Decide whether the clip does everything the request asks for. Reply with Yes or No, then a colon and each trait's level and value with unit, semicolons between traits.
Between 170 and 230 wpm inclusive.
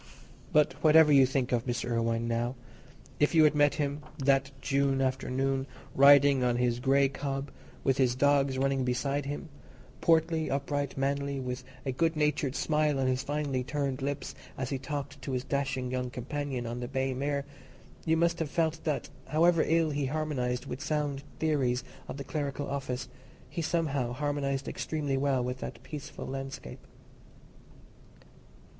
No: average, 160 wpm